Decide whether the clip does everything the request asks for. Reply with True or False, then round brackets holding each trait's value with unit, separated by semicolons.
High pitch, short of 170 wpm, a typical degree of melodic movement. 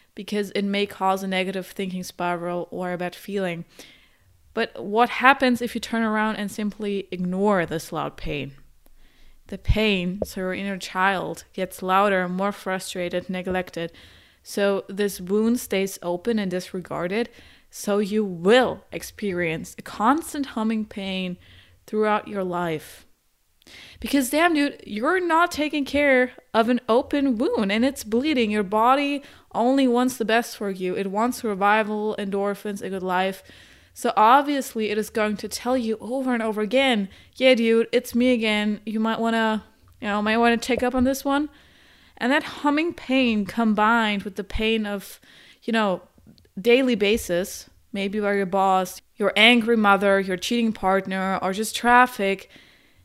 True (210 Hz; 160 wpm; 3.8 semitones)